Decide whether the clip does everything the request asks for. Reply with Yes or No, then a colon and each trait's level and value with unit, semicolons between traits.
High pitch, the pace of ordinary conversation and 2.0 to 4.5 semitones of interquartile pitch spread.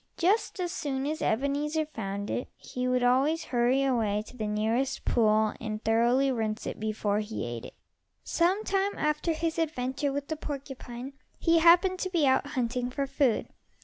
No: very high, 265 Hz; average, 175 wpm; wide, 5.4 semitones